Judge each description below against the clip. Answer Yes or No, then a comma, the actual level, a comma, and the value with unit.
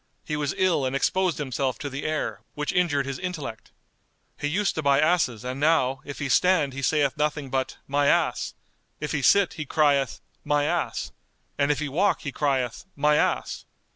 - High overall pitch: No, medium, 145 Hz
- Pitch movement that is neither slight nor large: No, narrow, 2.3 semitones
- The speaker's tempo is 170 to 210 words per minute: Yes, average, 190 wpm